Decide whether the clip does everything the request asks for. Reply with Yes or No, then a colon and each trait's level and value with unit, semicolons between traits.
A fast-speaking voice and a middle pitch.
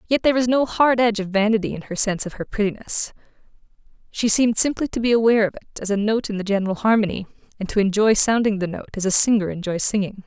No: fast, 235 wpm; high, 210 Hz